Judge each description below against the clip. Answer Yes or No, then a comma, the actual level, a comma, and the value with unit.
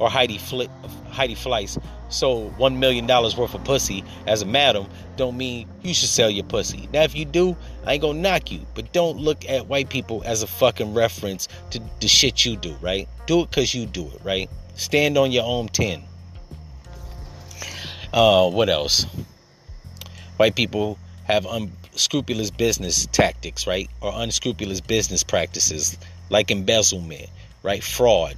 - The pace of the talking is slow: No, average, 165 wpm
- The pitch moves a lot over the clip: Yes, wide, 6.1 semitones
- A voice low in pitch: Yes, low, 105 Hz